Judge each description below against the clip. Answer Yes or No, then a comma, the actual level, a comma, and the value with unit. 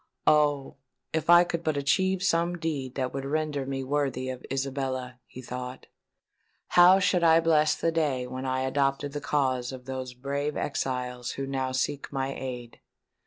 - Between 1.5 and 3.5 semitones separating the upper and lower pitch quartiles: Yes, average, 2.9 semitones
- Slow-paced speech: No, average, 165 wpm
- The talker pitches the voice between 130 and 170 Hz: Yes, low, 135 Hz